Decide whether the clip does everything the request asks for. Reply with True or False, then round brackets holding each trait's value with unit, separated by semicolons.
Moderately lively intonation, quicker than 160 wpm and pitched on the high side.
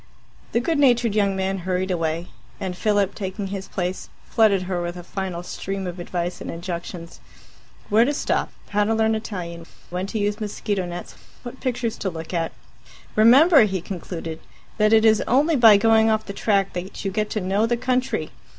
True (3.6 semitones; 185 wpm; 200 Hz)